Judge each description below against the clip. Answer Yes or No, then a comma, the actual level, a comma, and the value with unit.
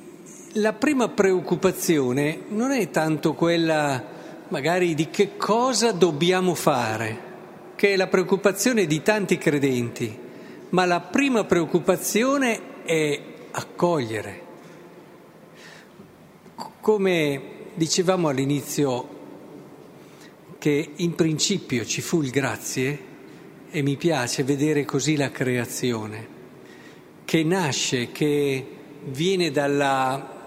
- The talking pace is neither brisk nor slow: No, slow, 95 wpm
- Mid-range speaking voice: Yes, medium, 165 Hz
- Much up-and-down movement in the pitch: No, average, 4.9 semitones